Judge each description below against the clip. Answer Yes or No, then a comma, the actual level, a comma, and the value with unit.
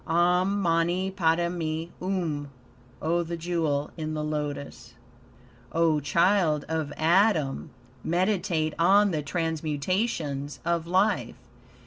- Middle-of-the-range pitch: Yes, medium, 165 Hz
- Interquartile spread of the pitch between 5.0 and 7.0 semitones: No, narrow, 2.6 semitones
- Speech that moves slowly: Yes, slow, 100 wpm